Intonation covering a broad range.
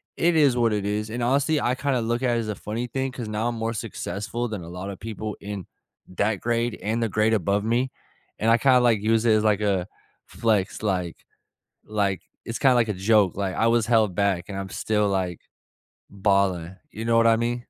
No: average, 2.9 semitones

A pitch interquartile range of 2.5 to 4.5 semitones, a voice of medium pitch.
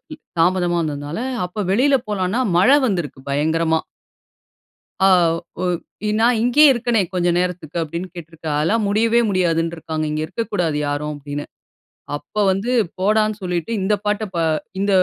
No: average, 4.9 semitones; medium, 180 Hz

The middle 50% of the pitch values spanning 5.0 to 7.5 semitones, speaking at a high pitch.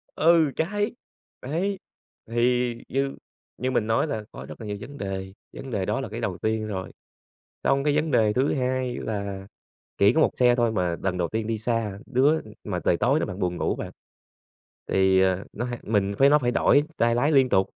No: average, 5.3 semitones; low, 120 Hz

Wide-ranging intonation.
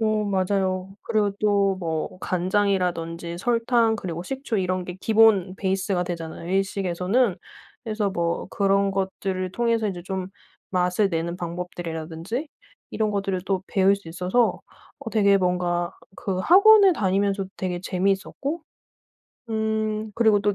No: average, 3.0 semitones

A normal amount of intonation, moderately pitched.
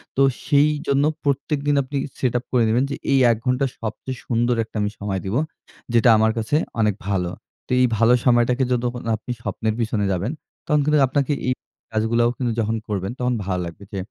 No: average, 3.4 semitones; low, 120 Hz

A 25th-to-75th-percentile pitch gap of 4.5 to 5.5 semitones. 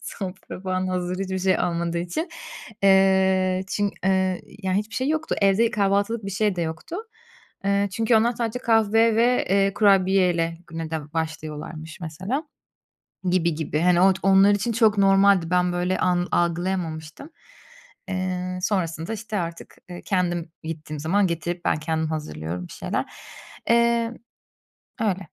No: average, 3.1 semitones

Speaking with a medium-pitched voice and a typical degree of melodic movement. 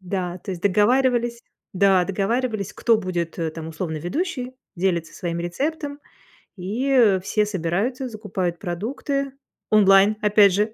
No: high, 200 Hz; average, 5.0 semitones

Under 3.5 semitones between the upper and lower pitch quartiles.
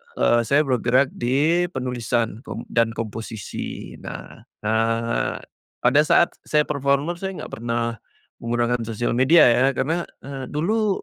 No: average, 4.1 semitones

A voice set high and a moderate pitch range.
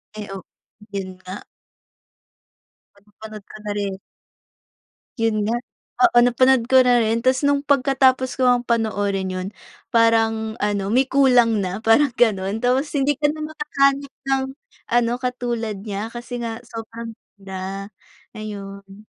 Yes: high, 230 Hz; average, 4.0 semitones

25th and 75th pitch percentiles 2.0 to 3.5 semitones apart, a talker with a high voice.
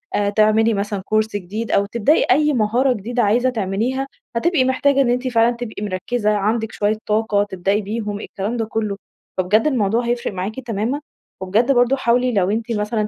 Yes: average, 3.0 semitones; high, 220 Hz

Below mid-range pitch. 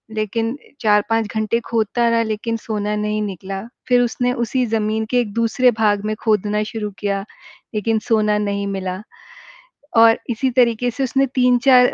No: high, 220 Hz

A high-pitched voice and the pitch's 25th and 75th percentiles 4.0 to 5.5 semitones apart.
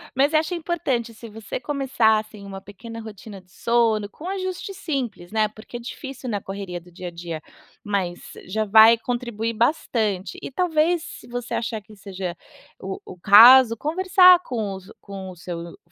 Yes: high, 225 Hz; average, 4.9 semitones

